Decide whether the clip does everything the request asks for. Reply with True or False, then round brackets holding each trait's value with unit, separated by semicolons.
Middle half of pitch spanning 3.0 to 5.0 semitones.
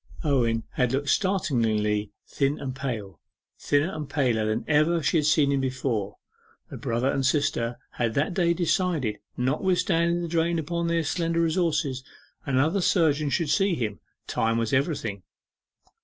False (5.6 semitones)